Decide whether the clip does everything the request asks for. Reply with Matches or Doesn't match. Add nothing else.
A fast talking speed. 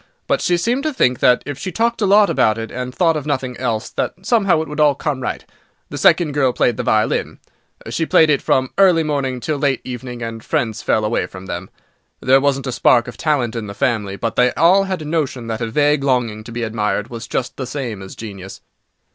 Matches